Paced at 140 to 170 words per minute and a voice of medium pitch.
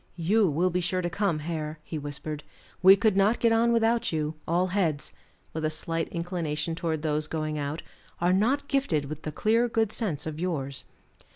No: average, 190 wpm; medium, 170 Hz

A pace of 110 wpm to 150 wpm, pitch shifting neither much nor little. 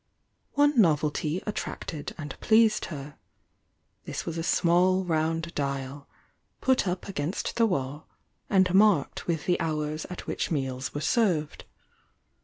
Yes: slow, 135 wpm; average, 4.2 semitones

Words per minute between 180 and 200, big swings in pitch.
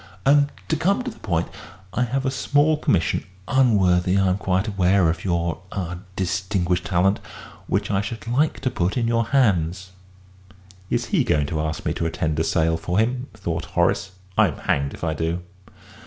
Yes: average, 185 wpm; wide, 5.8 semitones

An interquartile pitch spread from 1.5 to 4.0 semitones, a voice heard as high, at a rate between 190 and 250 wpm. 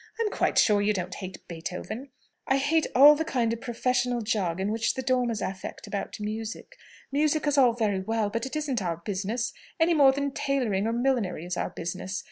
No: wide, 5.4 semitones; high, 230 Hz; average, 195 wpm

